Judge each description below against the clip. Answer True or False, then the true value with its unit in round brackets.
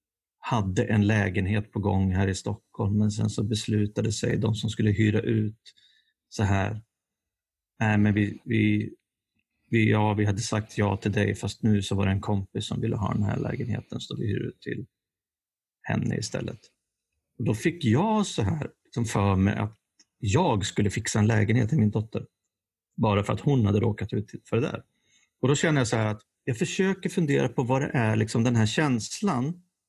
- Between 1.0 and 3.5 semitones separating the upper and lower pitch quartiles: True (2.4 semitones)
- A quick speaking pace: True (200 wpm)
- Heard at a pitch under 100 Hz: False (110 Hz)